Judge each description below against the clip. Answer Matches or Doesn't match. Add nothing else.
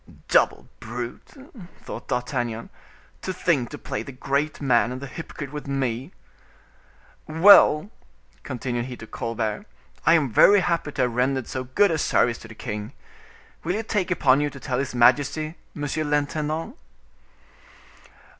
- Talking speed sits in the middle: Matches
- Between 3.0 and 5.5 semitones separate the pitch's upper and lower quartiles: Matches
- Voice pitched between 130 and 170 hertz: Matches